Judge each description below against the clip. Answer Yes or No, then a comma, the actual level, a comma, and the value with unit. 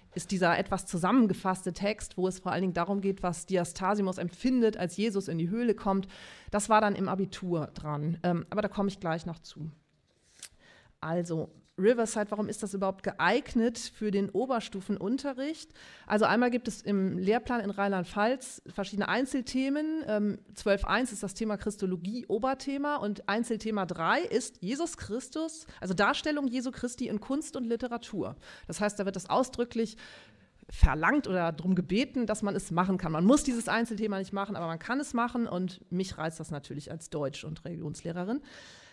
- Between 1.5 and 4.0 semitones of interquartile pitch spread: No, average, 4.6 semitones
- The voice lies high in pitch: Yes, high, 205 Hz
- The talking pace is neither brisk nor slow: Yes, average, 170 wpm